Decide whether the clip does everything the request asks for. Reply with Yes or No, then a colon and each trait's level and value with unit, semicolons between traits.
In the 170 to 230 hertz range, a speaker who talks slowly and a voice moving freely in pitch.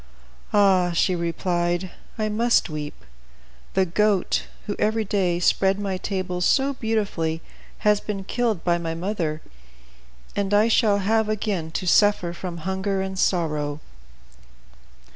No: high, 190 Hz; slow, 130 wpm; average, 3.3 semitones